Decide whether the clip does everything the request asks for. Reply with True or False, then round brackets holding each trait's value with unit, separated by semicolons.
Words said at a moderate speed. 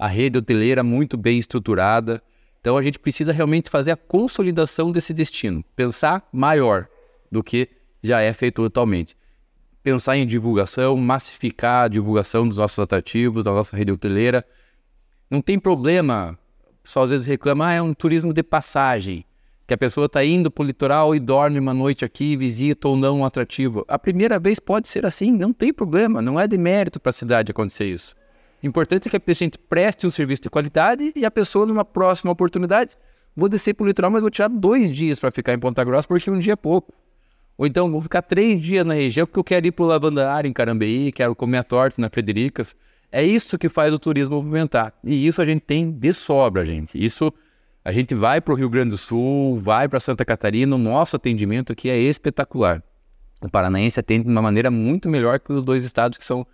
False (205 wpm)